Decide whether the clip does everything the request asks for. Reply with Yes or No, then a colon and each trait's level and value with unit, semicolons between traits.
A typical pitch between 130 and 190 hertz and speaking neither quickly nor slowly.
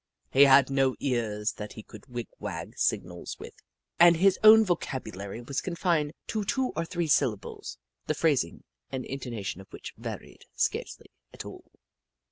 Yes: low, 135 Hz; average, 160 wpm